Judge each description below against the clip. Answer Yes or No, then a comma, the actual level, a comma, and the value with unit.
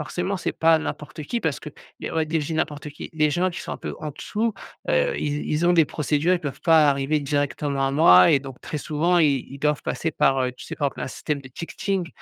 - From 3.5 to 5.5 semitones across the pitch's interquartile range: No, average, 2.9 semitones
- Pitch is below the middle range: No, medium, 150 Hz